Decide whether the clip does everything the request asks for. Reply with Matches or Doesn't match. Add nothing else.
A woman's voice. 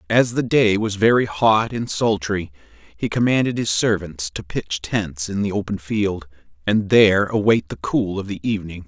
Doesn't match